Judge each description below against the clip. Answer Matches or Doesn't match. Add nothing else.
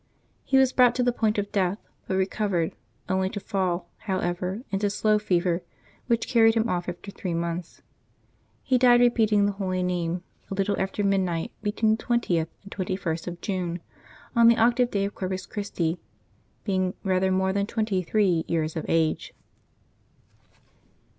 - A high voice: Matches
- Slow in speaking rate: Doesn't match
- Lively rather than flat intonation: Doesn't match